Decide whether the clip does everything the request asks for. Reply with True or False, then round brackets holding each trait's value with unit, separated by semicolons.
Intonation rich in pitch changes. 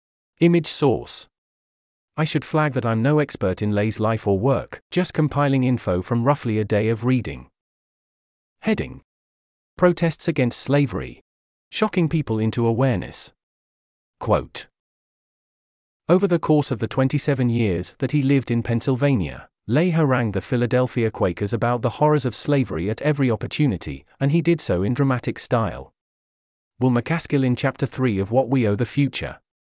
True (6.7 semitones)